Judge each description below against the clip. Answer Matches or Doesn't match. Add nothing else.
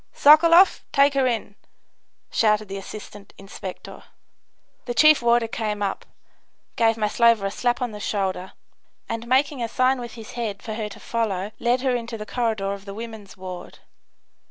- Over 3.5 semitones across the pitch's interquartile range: Doesn't match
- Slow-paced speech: Doesn't match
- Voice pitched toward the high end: Matches